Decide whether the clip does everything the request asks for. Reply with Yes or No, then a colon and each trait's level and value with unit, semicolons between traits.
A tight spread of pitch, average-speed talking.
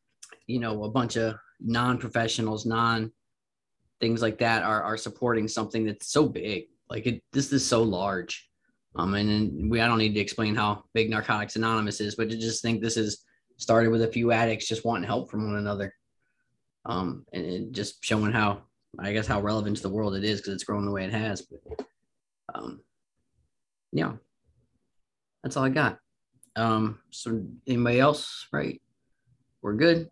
Yes: narrow, 1.7 semitones; average, 175 wpm